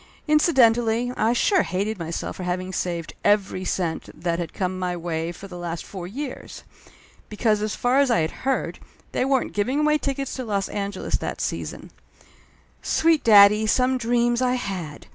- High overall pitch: Yes, high, 210 Hz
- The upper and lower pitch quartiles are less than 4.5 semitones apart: No, wide, 5.6 semitones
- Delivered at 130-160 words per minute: No, average, 175 wpm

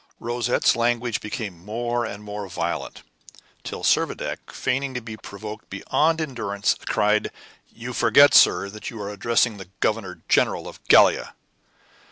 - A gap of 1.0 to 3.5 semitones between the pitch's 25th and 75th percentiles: Yes, average, 2.8 semitones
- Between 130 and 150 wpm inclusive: Yes, average, 140 wpm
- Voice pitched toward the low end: Yes, low, 110 Hz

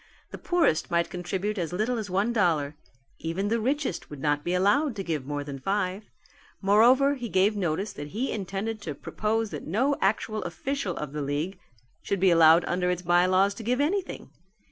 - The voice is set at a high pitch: Yes, high, 195 Hz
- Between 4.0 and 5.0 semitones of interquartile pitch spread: Yes, average, 4.6 semitones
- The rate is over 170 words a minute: Yes, average, 190 wpm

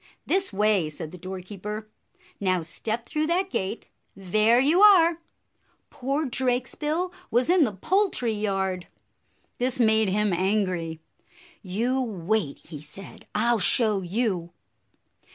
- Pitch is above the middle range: Yes, high, 215 Hz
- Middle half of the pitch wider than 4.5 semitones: Yes, wide, 5.6 semitones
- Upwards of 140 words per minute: No, slow, 135 wpm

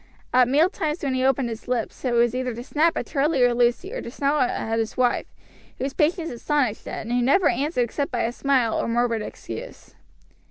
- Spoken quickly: Yes, fast, 210 wpm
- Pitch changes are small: No, average, 3.4 semitones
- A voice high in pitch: Yes, very high, 255 Hz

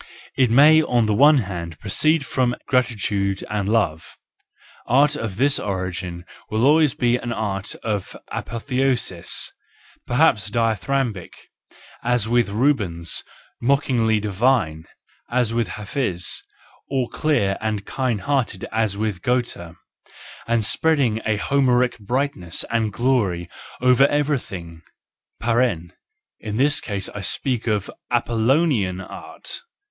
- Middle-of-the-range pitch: No, low, 115 Hz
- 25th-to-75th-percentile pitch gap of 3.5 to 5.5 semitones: Yes, average, 4.8 semitones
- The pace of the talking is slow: Yes, slow, 110 wpm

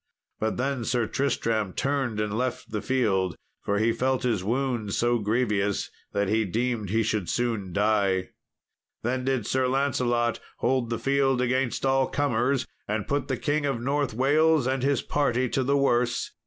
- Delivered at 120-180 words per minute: Yes, average, 170 wpm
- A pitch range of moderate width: Yes, average, 3.5 semitones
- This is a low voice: Yes, low, 120 Hz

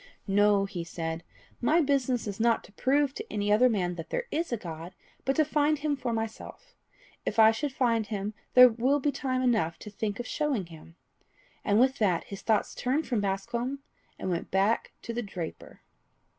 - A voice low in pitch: No, high, 225 Hz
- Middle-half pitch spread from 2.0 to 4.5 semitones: No, average, 5.1 semitones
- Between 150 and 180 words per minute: No, average, 195 wpm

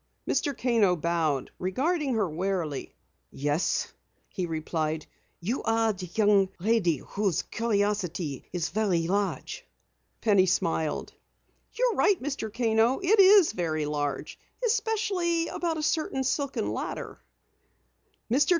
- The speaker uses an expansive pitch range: Yes, wide, 8.1 semitones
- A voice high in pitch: Yes, high, 205 Hz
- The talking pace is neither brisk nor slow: No, slow, 120 wpm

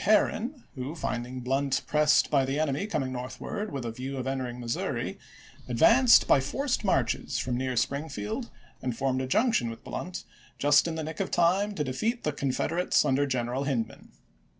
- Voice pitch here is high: No, medium, 140 Hz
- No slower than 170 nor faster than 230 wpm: Yes, average, 175 wpm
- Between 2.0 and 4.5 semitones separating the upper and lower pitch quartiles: No, average, 4.9 semitones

